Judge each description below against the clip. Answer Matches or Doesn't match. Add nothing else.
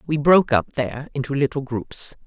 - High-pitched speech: Doesn't match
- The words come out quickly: Doesn't match